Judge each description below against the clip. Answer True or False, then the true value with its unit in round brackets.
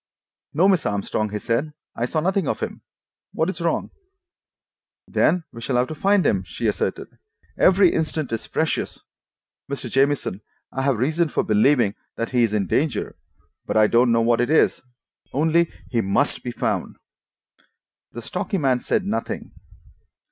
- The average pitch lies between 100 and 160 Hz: True (135 Hz)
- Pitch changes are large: True (5.8 semitones)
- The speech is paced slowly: False (160 wpm)